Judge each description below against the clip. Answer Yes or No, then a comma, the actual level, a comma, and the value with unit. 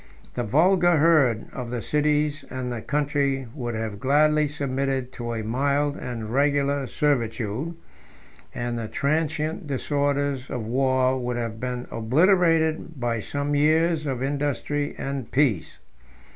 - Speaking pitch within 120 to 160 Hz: Yes, medium, 140 Hz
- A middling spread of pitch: Yes, average, 3.4 semitones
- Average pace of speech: No, slow, 130 wpm